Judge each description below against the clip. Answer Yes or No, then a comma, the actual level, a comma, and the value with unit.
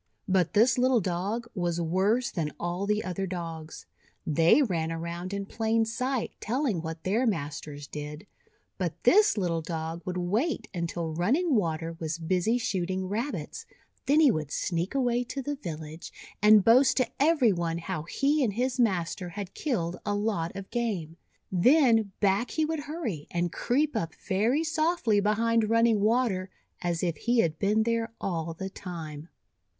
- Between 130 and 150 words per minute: No, average, 165 wpm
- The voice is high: Yes, high, 195 Hz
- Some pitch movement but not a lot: No, wide, 5.8 semitones